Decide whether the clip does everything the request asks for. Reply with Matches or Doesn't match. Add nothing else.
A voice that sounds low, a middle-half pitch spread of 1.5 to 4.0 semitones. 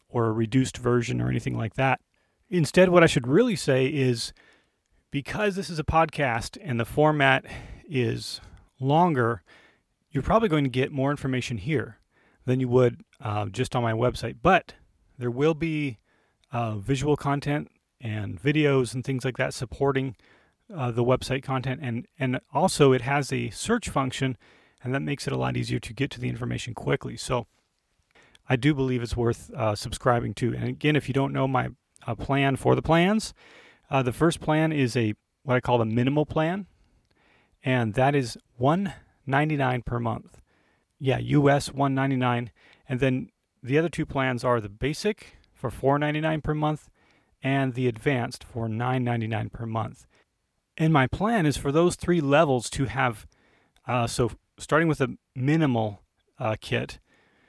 Matches